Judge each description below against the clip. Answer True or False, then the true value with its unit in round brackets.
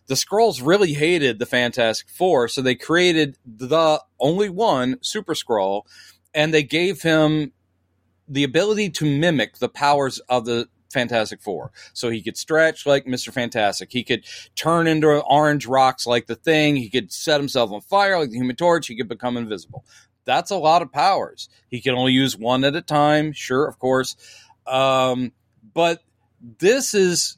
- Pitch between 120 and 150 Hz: True (135 Hz)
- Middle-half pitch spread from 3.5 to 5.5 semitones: True (4.6 semitones)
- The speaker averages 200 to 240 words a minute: False (175 wpm)